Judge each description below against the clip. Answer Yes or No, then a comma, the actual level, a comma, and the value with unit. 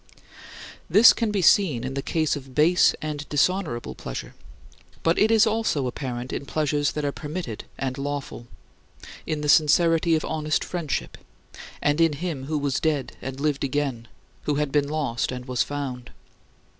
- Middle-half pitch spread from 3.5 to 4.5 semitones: No, average, 2.9 semitones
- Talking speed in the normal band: Yes, average, 170 wpm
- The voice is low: No, medium, 145 Hz